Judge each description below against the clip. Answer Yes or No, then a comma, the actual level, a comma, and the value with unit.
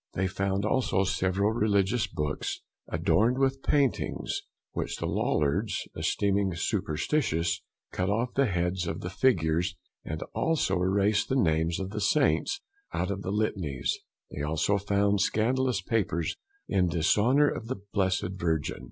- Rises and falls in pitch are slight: No, average, 3.7 semitones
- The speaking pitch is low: Yes, very low, 95 Hz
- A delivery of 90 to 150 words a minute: Yes, average, 140 wpm